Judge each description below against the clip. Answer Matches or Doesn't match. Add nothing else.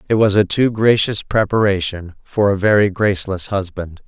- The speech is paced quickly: Doesn't match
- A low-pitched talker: Matches